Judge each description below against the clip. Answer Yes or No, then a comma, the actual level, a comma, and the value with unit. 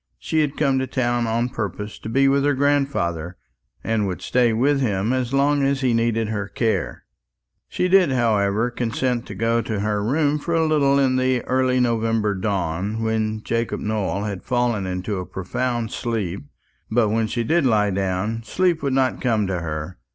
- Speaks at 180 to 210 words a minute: Yes, average, 185 wpm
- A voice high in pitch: No, low, 115 Hz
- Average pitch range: Yes, average, 4.0 semitones